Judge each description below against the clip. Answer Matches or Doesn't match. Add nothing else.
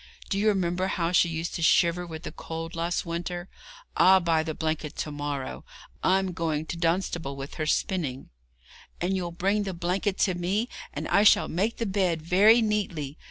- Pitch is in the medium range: Matches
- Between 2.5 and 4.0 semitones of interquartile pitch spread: Matches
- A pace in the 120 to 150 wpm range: Doesn't match